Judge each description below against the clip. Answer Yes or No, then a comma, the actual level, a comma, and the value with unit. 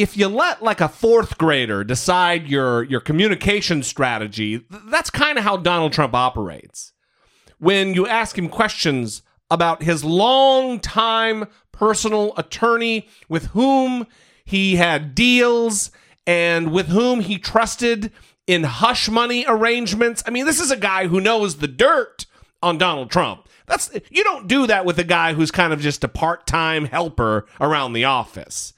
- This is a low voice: No, medium, 185 Hz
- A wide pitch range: Yes, wide, 6.2 semitones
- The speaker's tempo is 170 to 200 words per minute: No, average, 155 wpm